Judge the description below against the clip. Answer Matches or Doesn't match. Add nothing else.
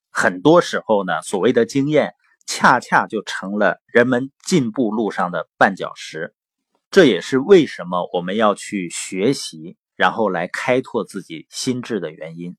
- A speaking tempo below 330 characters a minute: Matches